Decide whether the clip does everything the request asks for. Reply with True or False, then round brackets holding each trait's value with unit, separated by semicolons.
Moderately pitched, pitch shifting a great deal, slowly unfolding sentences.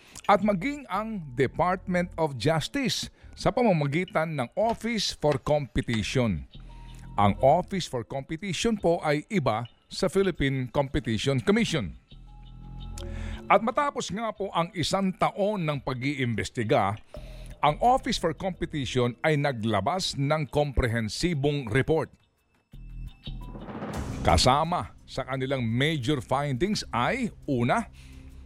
True (145 Hz; 6.0 semitones; 100 wpm)